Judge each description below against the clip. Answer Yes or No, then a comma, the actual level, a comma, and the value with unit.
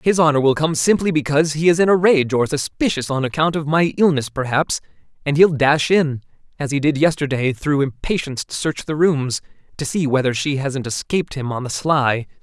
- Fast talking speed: Yes, fast, 210 wpm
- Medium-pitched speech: Yes, medium, 145 Hz